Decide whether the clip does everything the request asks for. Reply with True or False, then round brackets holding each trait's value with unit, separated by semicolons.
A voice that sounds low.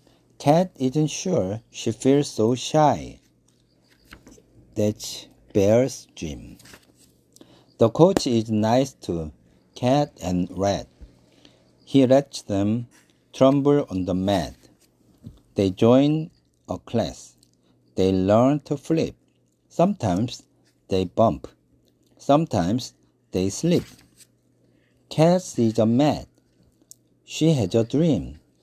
True (110 Hz)